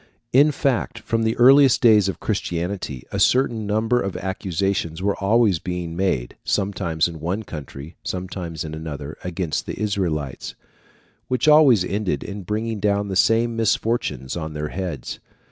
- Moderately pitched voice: No, very low, 95 Hz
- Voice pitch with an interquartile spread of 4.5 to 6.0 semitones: Yes, average, 5.2 semitones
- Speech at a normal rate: Yes, average, 150 wpm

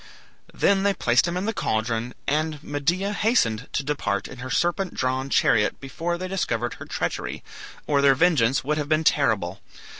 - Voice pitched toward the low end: No, medium, 145 Hz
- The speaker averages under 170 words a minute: No, average, 175 wpm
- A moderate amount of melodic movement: No, wide, 6.1 semitones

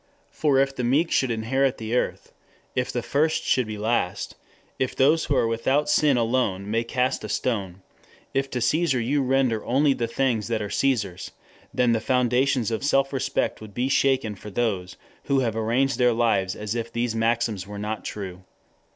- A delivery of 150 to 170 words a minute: No, average, 190 wpm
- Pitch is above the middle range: No, low, 120 Hz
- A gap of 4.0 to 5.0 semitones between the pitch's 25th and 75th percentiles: No, average, 3.5 semitones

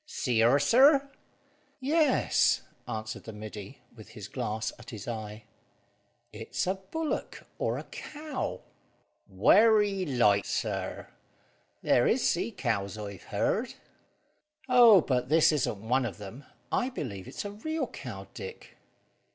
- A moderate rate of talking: No, slow, 130 wpm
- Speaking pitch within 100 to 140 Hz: Yes, low, 135 Hz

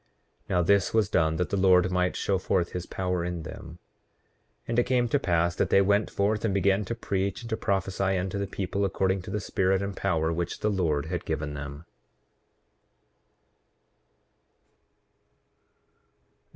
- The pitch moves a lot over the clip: No, narrow, 2.4 semitones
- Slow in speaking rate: No, average, 165 wpm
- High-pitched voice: No, very low, 95 Hz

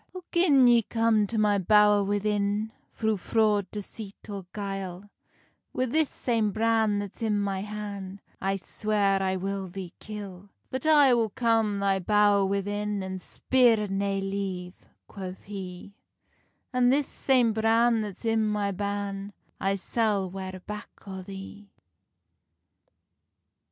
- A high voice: Yes, high, 205 Hz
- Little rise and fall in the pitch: Yes, narrow, 2.2 semitones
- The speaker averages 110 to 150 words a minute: Yes, slow, 135 wpm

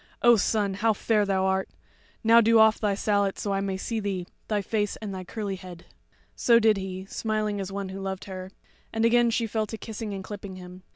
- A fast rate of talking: Yes, fast, 220 wpm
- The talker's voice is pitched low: No, high, 205 Hz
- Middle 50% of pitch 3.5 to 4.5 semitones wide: No, narrow, 2.4 semitones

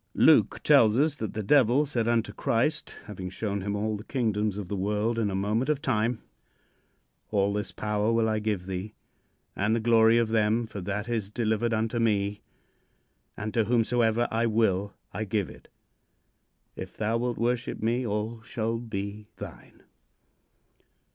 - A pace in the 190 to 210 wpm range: No, average, 165 wpm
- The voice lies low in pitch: Yes, low, 110 Hz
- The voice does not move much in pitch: Yes, narrow, 2.1 semitones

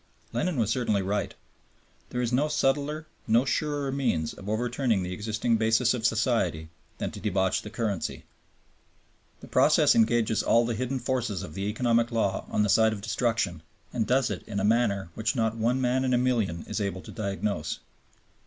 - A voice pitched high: No, low, 115 Hz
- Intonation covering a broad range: No, average, 3.5 semitones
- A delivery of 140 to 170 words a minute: No, average, 180 wpm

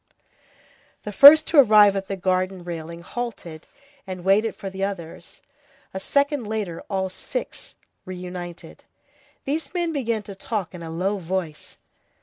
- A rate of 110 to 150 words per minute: Yes, average, 145 wpm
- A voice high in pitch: Yes, high, 195 Hz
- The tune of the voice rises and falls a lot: No, average, 3.9 semitones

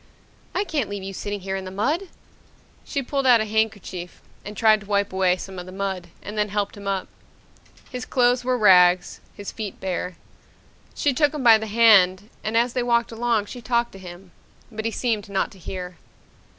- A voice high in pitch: Yes, high, 210 Hz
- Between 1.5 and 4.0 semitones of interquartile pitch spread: Yes, average, 3.7 semitones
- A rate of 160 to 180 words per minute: No, fast, 205 wpm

